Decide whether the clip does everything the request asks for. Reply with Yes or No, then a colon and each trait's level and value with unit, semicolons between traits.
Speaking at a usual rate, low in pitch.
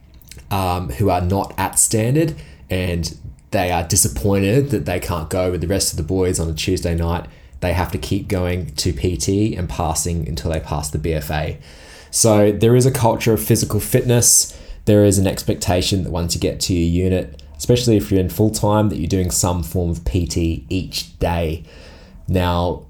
Yes: average, 190 wpm; very low, 90 Hz